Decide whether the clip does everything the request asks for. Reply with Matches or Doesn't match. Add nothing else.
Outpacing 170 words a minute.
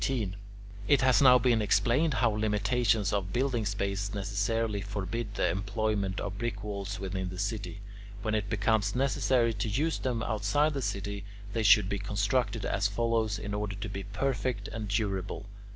Doesn't match